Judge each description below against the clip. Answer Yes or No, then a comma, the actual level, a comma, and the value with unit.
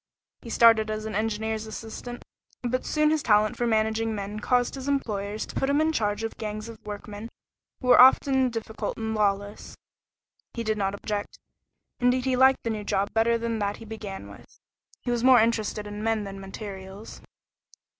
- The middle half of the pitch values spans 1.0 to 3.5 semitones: Yes, narrow, 2.6 semitones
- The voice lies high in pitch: Yes, high, 220 Hz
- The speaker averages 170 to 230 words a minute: Yes, average, 185 wpm